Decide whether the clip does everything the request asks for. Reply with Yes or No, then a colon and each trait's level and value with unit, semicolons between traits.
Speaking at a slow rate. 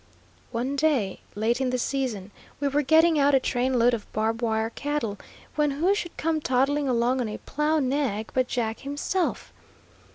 No: average, 175 wpm